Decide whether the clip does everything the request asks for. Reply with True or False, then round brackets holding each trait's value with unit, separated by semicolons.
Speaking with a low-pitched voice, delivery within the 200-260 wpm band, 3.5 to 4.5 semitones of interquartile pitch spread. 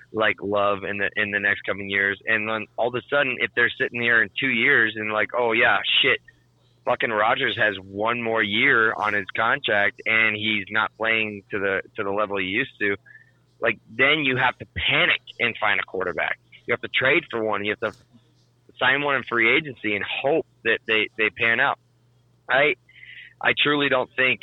False (110 Hz; 205 wpm; 2.8 semitones)